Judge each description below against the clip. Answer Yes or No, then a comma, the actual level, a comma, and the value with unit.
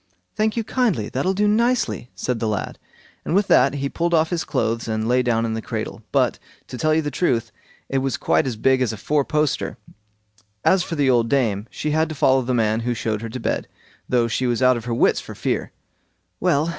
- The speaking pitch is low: Yes, low, 130 Hz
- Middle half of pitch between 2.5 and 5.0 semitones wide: No, wide, 5.4 semitones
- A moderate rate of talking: No, fast, 230 wpm